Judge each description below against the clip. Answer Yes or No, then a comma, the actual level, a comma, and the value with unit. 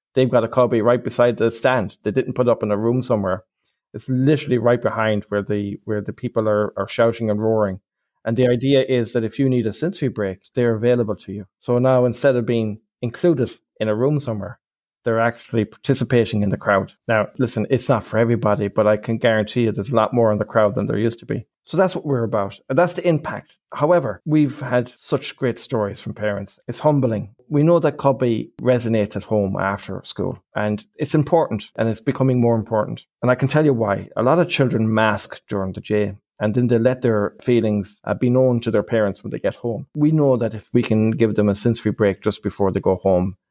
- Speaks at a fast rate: Yes, fast, 225 wpm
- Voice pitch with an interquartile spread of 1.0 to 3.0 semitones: No, average, 3.4 semitones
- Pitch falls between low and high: No, low, 115 Hz